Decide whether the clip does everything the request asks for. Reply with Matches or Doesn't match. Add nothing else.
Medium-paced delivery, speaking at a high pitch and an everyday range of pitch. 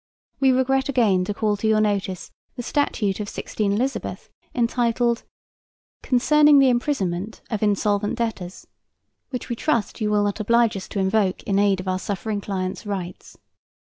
Matches